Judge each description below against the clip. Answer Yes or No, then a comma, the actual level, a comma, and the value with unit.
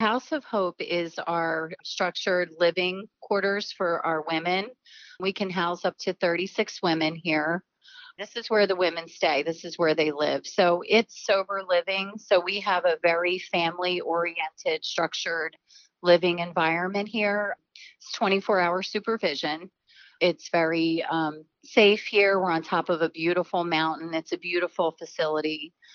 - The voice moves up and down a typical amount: Yes, average, 3.3 semitones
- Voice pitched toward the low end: No, medium, 180 Hz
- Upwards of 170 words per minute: No, average, 150 wpm